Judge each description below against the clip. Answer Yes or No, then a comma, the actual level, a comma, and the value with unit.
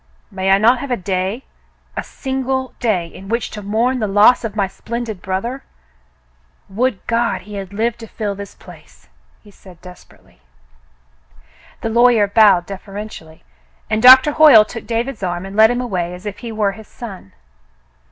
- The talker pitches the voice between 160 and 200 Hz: No, high, 215 Hz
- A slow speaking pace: No, average, 180 wpm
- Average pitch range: Yes, average, 3.6 semitones